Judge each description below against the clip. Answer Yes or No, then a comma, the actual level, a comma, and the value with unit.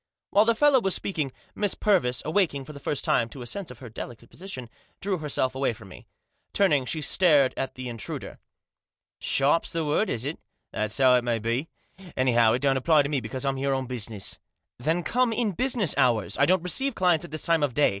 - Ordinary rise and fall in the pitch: No, wide, 6.2 semitones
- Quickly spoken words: Yes, fast, 225 wpm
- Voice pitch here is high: No, medium, 140 Hz